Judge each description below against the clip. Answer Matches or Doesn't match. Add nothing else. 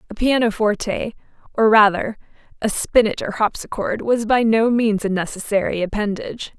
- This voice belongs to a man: Doesn't match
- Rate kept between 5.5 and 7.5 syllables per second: Doesn't match